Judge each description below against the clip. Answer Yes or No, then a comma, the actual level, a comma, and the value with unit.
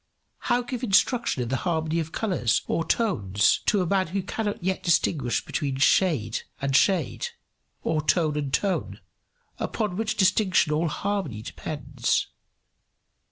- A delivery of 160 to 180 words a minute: No, average, 140 wpm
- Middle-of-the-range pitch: Yes, medium, 170 Hz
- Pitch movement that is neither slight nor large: No, wide, 5.8 semitones